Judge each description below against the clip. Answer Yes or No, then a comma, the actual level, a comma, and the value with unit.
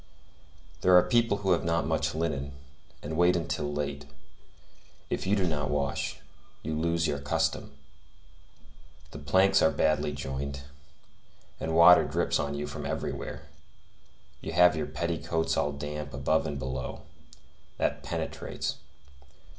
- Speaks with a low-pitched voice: Yes, very low, 80 Hz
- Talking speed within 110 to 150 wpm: Yes, slow, 135 wpm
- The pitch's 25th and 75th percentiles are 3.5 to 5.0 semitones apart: No, average, 2.9 semitones